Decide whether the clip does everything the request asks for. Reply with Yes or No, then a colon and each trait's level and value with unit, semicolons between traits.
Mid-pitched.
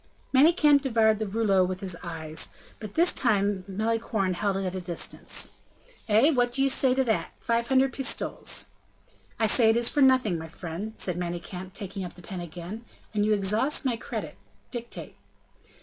No: high, 215 Hz